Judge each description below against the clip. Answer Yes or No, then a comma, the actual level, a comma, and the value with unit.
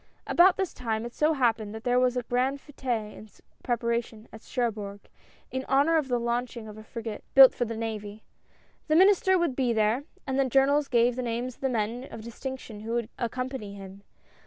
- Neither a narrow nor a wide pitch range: Yes, average, 3.2 semitones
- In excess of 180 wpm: Yes, fast, 205 wpm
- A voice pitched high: Yes, high, 240 Hz